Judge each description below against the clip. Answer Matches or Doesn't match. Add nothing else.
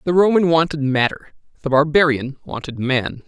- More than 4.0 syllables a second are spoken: Matches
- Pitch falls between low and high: Matches